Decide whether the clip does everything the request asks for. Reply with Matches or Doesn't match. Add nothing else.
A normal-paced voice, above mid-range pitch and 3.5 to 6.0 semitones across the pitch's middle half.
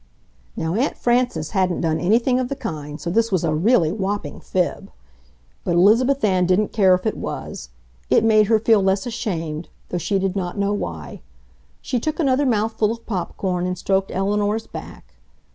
Matches